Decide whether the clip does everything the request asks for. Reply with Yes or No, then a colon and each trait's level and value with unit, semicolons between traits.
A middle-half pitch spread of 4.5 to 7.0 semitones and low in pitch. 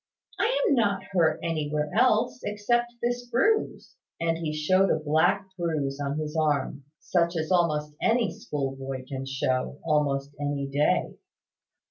No: average, 5.3 semitones; medium, 155 Hz